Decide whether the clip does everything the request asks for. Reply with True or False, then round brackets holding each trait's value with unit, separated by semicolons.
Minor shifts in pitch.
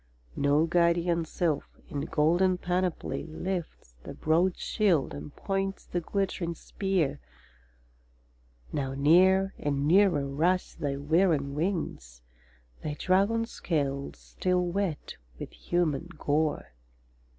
False (4.3 semitones)